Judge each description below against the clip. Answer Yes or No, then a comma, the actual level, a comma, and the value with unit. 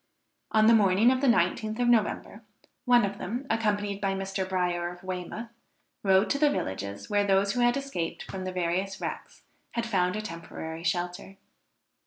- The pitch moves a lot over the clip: No, average, 3.9 semitones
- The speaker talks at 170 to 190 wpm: Yes, average, 175 wpm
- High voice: Yes, high, 195 Hz